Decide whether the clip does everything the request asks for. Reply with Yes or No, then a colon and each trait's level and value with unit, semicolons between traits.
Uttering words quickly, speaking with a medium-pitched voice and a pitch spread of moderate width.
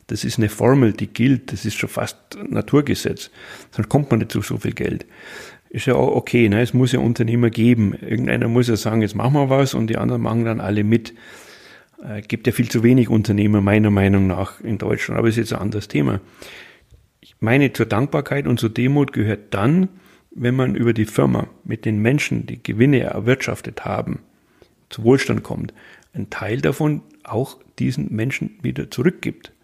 No: fast, 195 wpm; low, 115 Hz; average, 3.0 semitones